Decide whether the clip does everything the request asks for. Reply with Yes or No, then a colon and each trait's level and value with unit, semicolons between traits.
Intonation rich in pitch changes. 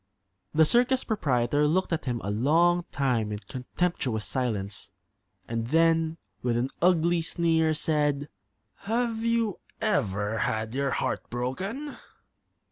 Yes: wide, 6.5 semitones